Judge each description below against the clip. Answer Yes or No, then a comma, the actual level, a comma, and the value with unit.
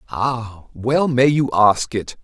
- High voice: No, low, 120 Hz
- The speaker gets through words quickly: No, average, 160 wpm